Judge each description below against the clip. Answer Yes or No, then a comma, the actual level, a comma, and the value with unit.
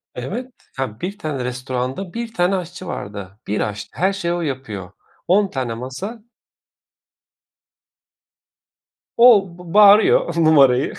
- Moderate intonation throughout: No, wide, 7.6 semitones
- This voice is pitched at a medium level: Yes, medium, 165 Hz